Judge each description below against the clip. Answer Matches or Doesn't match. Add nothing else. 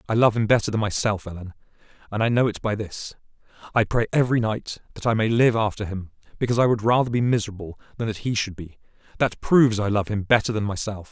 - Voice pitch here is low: Matches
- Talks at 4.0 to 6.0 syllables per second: Doesn't match